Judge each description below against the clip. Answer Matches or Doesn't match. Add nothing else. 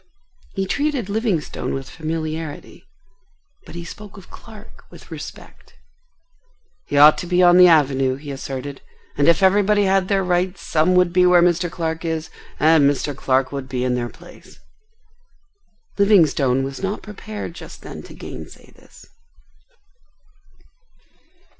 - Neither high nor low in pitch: Matches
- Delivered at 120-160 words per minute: Matches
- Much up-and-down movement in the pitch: Doesn't match